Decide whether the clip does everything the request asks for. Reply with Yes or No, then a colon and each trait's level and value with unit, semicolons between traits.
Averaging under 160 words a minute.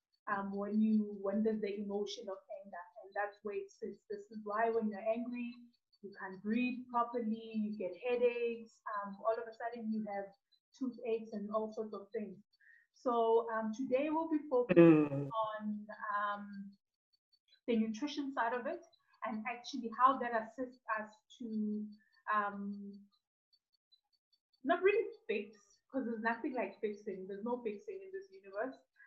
Yes: average, 150 wpm